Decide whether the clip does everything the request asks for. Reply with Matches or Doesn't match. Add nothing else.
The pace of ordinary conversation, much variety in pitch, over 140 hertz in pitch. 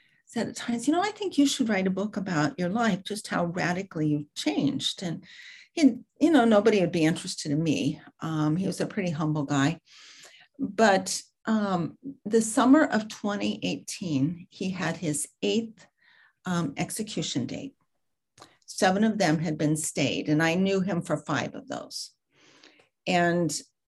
Matches